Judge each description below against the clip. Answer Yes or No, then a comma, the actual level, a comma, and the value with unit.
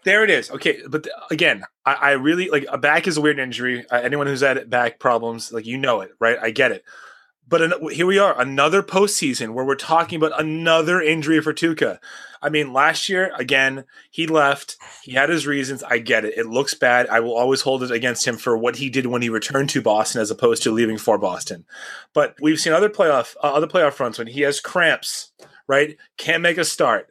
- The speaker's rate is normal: No, fast, 225 wpm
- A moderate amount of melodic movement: Yes, average, 4.4 semitones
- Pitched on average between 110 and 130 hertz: No, medium, 140 Hz